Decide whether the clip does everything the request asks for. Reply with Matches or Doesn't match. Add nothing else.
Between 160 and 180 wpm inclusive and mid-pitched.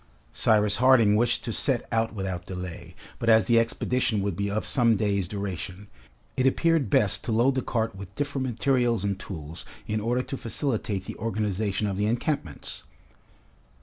Doesn't match